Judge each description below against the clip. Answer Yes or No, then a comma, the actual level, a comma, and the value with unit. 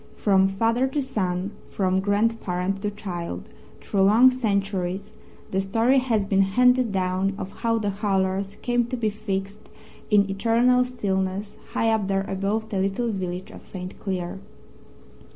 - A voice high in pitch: Yes, high, 200 Hz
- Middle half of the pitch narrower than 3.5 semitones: Yes, average, 2.9 semitones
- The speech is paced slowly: No, average, 150 wpm